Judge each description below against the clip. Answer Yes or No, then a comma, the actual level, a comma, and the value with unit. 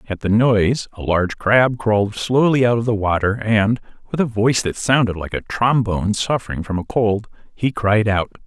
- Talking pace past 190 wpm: Yes, average, 200 wpm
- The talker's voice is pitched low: Yes, low, 110 Hz